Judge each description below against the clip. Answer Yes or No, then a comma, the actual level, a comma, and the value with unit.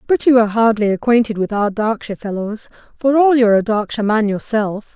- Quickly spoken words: No, average, 195 wpm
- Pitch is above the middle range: Yes, high, 220 Hz